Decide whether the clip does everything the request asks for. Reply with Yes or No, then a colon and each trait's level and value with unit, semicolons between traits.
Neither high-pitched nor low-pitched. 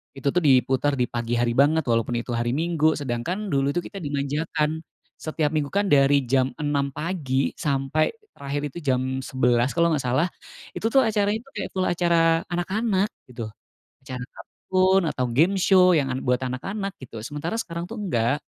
Yes: medium, 145 Hz